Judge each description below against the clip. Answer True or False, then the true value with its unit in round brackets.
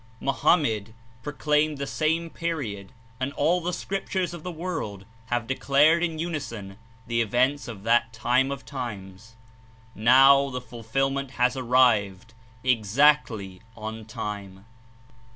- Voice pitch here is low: True (130 Hz)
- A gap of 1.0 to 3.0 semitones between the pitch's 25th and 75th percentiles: False (5.1 semitones)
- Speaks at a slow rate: True (125 wpm)